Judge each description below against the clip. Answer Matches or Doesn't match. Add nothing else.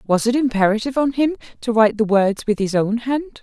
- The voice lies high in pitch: Matches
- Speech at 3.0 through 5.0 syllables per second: Doesn't match